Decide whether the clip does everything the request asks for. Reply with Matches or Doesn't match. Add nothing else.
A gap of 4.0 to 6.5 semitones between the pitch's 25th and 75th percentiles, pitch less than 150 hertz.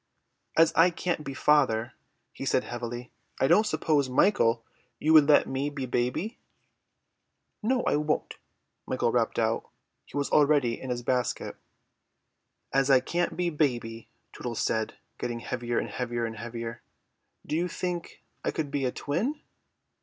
Matches